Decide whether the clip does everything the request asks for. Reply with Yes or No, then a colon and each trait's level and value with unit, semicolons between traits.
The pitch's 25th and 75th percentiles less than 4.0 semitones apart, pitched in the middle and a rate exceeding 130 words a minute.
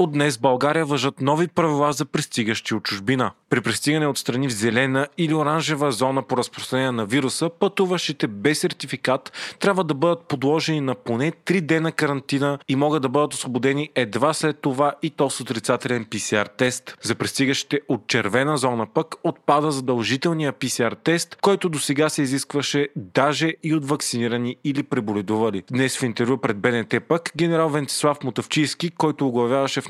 Yes: average, 3.4 semitones; medium, 145 Hz; average, 160 wpm